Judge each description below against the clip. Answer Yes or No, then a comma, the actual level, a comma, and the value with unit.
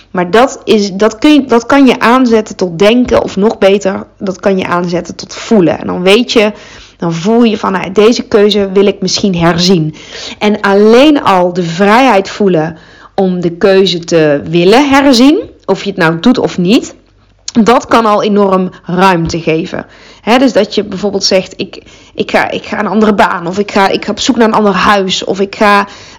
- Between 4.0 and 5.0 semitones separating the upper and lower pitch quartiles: No, average, 3.3 semitones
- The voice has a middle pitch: No, high, 200 Hz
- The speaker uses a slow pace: No, fast, 200 wpm